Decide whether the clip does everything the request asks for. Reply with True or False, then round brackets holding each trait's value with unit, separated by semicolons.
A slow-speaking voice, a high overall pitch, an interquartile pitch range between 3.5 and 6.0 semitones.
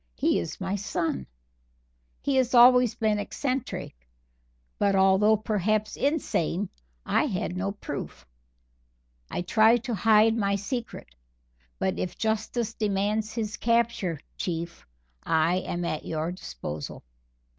True (120 wpm; 205 Hz; 4.1 semitones)